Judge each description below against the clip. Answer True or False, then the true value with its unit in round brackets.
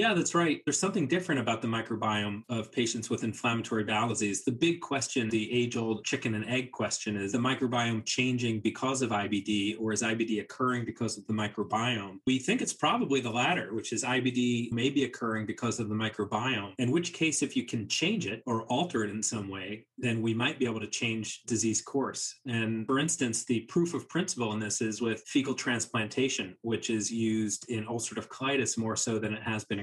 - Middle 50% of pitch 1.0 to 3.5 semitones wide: True (2.8 semitones)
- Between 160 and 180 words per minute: False (205 wpm)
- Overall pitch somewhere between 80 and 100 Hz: False (115 Hz)